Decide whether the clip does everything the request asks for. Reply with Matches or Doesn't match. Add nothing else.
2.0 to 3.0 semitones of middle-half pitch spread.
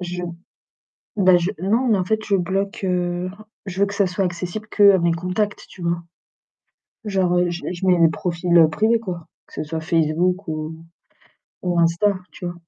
Matches